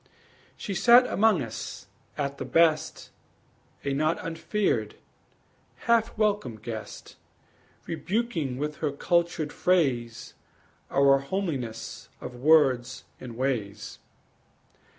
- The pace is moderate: No, slow, 95 wpm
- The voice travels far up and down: Yes, wide, 6.0 semitones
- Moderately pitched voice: Yes, medium, 150 Hz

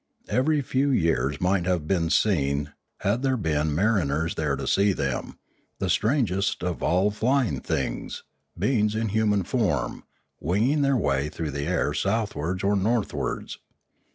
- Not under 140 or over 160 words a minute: Yes, average, 145 wpm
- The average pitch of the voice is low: Yes, very low, 95 Hz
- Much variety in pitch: Yes, wide, 6.2 semitones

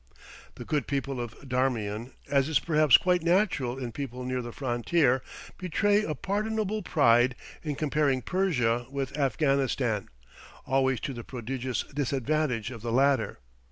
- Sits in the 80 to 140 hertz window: Yes, low, 135 Hz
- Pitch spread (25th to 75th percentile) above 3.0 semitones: Yes, average, 3.8 semitones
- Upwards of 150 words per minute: No, average, 140 wpm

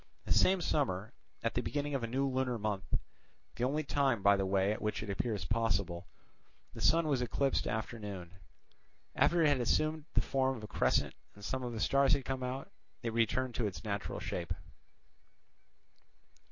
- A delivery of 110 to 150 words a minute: No, average, 185 wpm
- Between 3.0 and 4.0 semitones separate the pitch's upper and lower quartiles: No, average, 4.9 semitones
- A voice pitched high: No, low, 120 Hz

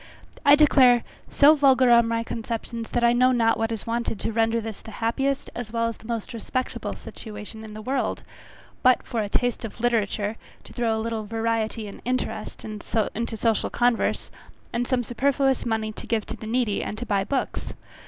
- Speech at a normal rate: Yes, average, 190 wpm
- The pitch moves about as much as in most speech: No, narrow, 1.8 semitones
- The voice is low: No, high, 230 Hz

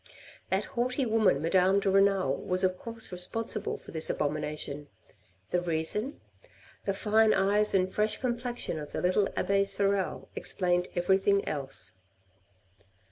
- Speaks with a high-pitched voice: Yes, high, 195 Hz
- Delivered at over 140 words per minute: No, slow, 135 wpm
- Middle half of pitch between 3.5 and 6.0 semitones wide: No, average, 3.1 semitones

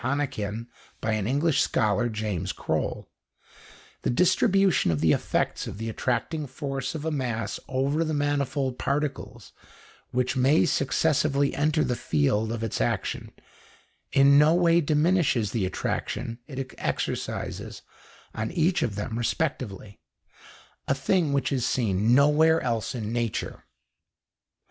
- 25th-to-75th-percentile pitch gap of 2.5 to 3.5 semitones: No, average, 5.0 semitones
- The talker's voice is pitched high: No, low, 135 Hz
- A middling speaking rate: No, slow, 130 wpm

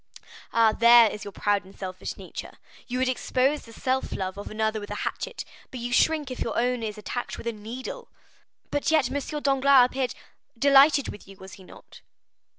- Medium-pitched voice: No, high, 245 Hz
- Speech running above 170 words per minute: Yes, average, 195 wpm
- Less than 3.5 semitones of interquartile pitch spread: No, average, 4.2 semitones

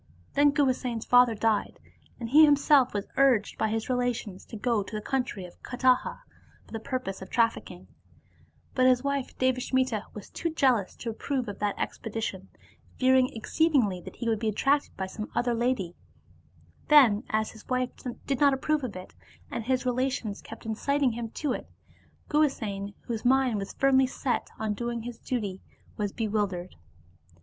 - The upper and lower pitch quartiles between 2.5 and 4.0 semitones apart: Yes, average, 3.6 semitones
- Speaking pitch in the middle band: No, high, 240 Hz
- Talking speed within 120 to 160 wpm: No, average, 170 wpm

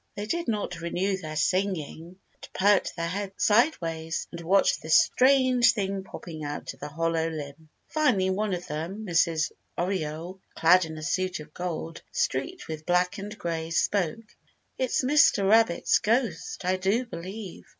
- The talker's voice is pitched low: No, medium, 185 Hz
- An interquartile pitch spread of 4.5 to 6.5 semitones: No, average, 4.1 semitones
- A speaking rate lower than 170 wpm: Yes, average, 160 wpm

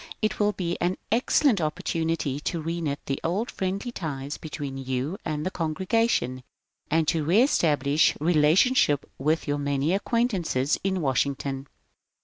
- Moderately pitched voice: Yes, medium, 160 Hz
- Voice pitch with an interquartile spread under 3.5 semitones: No, average, 4.8 semitones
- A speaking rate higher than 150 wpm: No, average, 140 wpm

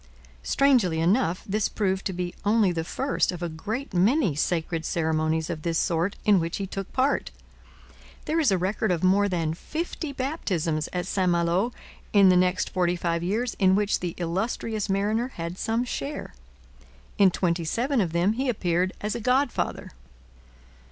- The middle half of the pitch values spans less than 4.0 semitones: No, average, 4.6 semitones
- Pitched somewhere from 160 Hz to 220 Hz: Yes, high, 190 Hz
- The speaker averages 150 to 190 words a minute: Yes, average, 170 wpm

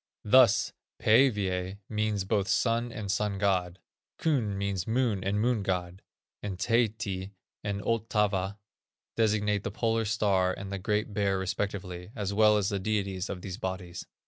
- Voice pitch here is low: Yes, low, 100 Hz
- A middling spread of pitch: No, narrow, 2.2 semitones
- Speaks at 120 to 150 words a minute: Yes, average, 145 wpm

